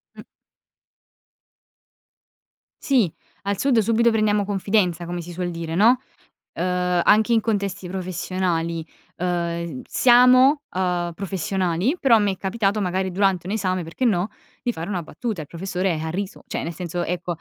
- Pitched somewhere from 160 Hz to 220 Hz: Yes, medium, 185 Hz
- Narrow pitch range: No, average, 3.4 semitones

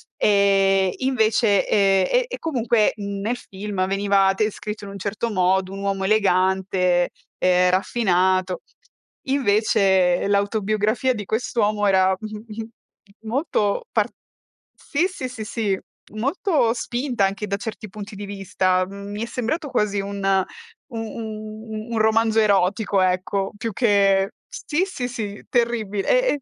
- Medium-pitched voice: No, high, 205 Hz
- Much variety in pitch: No, average, 2.7 semitones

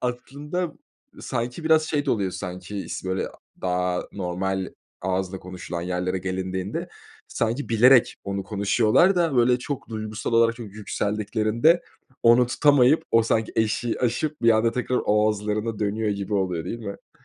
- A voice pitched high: No, low, 110 Hz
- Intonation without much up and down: No, average, 4.3 semitones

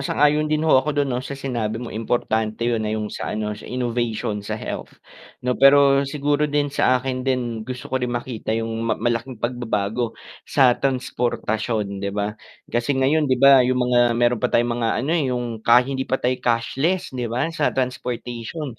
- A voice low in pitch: Yes, low, 125 Hz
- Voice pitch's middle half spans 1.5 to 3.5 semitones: Yes, average, 2.8 semitones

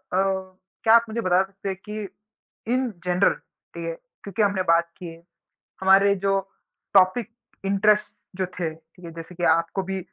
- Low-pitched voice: No, high, 190 Hz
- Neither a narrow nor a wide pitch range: No, narrow, 2.0 semitones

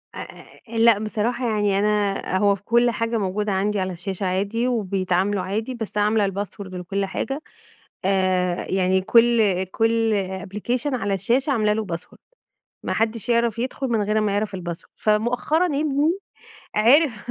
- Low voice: No, high, 210 Hz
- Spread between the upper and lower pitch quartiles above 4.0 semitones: No, average, 3.2 semitones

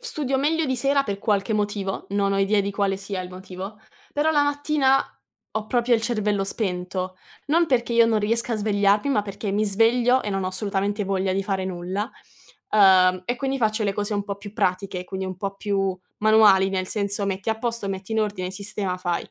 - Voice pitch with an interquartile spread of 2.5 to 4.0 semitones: Yes, average, 2.9 semitones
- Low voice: No, high, 205 Hz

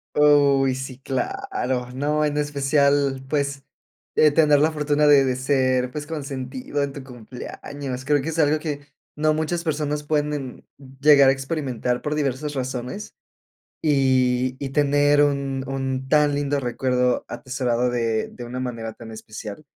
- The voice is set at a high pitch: No, medium, 140 Hz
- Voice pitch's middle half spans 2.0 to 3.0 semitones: Yes, narrow, 2.4 semitones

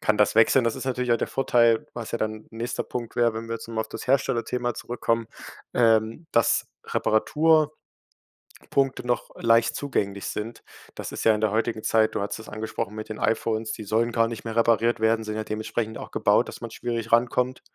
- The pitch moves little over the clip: Yes, narrow, 1.5 semitones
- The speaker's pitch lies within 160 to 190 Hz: No, low, 115 Hz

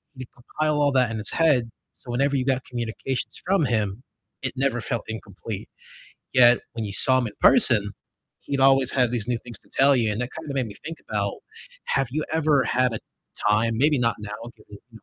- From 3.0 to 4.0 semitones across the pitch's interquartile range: Yes, average, 3.3 semitones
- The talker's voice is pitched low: Yes, low, 125 Hz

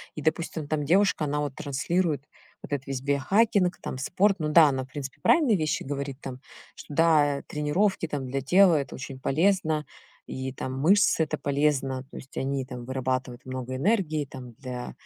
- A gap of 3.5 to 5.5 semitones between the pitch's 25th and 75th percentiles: Yes, average, 3.8 semitones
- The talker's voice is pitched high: No, medium, 145 Hz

